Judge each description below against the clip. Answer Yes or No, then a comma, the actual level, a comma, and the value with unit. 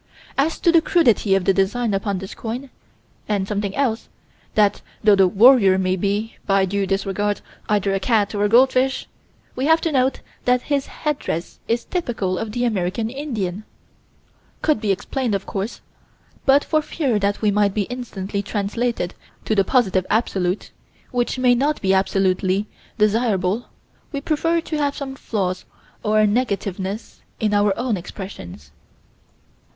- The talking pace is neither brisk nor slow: Yes, average, 155 wpm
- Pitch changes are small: No, average, 4.4 semitones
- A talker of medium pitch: No, high, 210 Hz